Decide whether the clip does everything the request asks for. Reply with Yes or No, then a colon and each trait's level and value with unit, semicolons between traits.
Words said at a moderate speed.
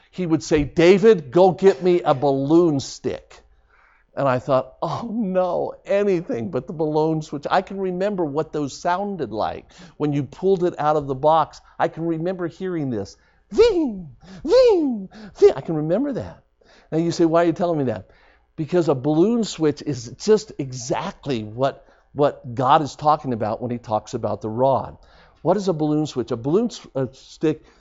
Yes: average, 180 wpm